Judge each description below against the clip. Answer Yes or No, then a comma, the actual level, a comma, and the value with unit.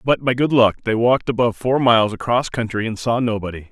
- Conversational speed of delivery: No, fast, 225 wpm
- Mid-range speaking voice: No, low, 115 Hz